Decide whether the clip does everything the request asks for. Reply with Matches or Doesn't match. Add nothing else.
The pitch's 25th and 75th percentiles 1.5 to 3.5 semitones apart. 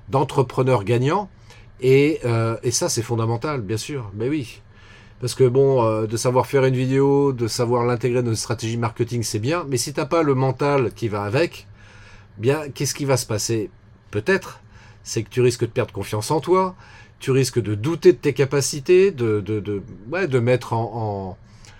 Doesn't match